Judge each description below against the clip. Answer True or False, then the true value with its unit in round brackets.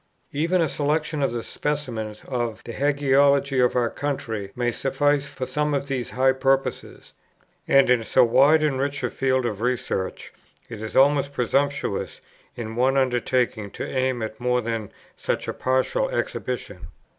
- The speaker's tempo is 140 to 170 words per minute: True (155 wpm)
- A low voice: True (130 Hz)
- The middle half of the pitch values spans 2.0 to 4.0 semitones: True (2.9 semitones)